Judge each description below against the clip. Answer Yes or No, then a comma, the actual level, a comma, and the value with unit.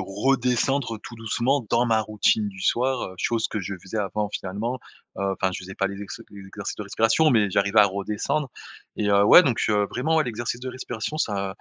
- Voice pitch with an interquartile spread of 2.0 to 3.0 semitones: No, average, 3.7 semitones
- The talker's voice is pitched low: Yes, low, 110 Hz